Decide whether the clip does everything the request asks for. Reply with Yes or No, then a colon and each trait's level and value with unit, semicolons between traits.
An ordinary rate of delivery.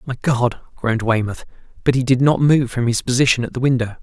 No: fast, 210 wpm